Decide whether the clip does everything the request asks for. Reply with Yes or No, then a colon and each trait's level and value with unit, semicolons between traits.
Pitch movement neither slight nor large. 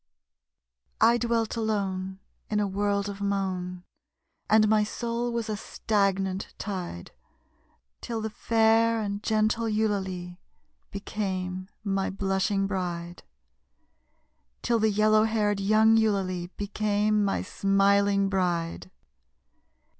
No: narrow, 2.1 semitones